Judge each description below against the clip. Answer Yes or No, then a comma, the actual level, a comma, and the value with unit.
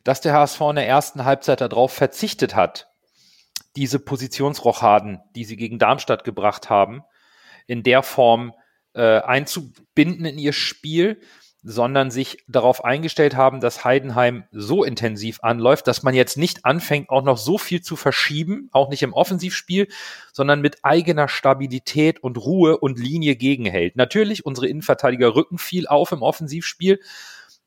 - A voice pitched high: No, low, 135 Hz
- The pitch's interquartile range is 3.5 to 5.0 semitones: Yes, average, 4.0 semitones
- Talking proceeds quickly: No, average, 145 wpm